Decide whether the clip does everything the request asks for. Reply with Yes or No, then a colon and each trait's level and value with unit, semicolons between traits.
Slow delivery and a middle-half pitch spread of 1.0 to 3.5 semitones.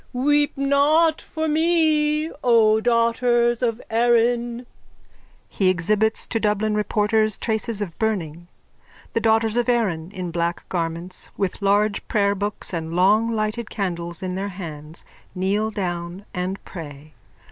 No: slow, 130 wpm; average, 4.5 semitones